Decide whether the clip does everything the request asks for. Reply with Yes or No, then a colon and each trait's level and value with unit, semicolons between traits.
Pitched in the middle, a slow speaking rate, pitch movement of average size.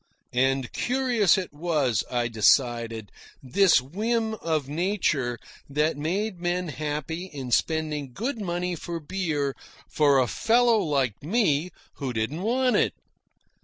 No: medium, 155 Hz; slow, 130 wpm; wide, 6.0 semitones